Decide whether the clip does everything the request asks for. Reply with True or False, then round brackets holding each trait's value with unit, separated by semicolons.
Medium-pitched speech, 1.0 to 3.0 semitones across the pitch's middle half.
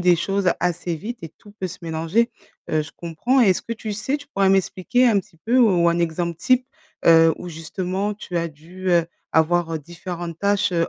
False (180 Hz; 3.5 semitones)